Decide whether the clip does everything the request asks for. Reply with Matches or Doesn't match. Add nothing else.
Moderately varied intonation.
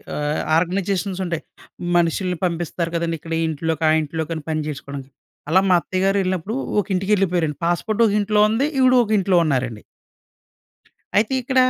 Matches